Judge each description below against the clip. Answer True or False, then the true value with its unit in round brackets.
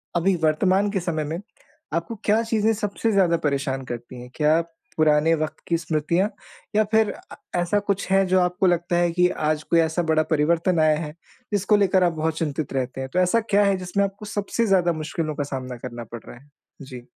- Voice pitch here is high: False (170 Hz)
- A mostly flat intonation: False (4.0 semitones)